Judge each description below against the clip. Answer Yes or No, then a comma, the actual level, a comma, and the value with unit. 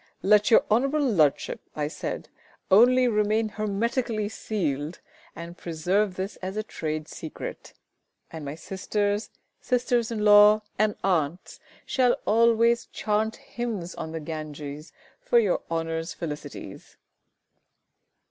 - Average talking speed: No, slow, 120 wpm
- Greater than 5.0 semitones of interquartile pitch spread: Yes, wide, 5.4 semitones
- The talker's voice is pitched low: No, high, 205 Hz